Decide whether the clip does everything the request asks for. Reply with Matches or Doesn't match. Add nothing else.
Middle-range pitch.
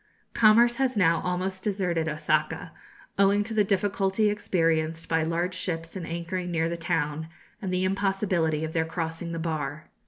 Matches